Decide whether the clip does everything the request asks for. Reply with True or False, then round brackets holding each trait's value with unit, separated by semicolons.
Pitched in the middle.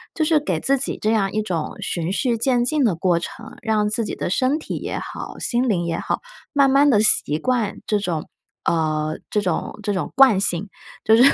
False (215 Hz)